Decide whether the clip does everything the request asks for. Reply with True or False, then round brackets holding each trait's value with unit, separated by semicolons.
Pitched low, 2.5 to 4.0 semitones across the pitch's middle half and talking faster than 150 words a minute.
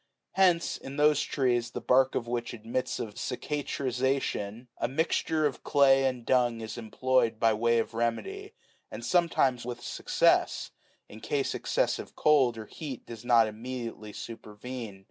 False (125 Hz; 2.9 semitones; 145 wpm)